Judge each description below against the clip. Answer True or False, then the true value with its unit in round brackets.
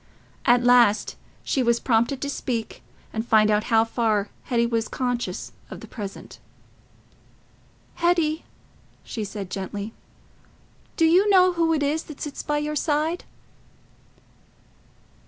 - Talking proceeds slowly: True (130 wpm)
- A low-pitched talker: False (245 Hz)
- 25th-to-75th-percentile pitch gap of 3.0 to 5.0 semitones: False (5.4 semitones)